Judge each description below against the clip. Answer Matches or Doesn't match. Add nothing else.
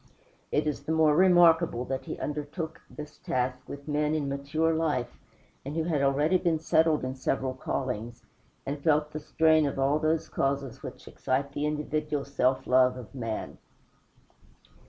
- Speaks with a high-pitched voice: Doesn't match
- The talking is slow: Doesn't match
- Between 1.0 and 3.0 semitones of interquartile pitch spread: Matches